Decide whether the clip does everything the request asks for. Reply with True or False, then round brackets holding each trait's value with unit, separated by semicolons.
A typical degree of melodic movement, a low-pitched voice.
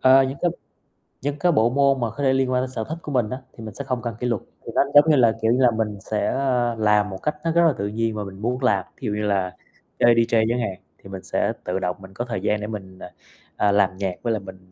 True (4.2 semitones; 115 Hz)